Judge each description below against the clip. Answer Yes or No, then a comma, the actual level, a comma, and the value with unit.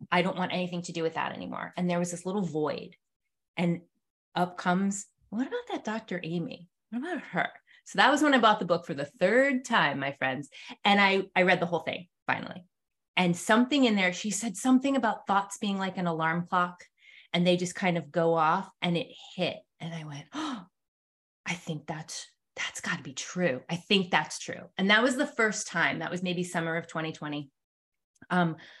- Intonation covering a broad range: No, average, 4.1 semitones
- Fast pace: Yes, fast, 210 wpm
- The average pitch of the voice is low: No, medium, 180 Hz